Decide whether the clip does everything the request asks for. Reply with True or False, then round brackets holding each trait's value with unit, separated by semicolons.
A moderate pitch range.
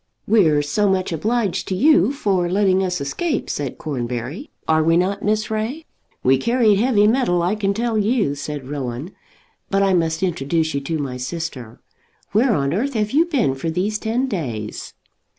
False (6.7 semitones)